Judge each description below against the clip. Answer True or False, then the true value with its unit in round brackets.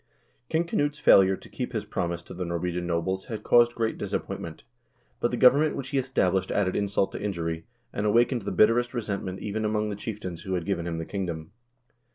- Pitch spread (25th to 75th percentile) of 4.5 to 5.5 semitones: True (5.0 semitones)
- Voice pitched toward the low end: True (100 Hz)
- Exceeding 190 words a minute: True (200 wpm)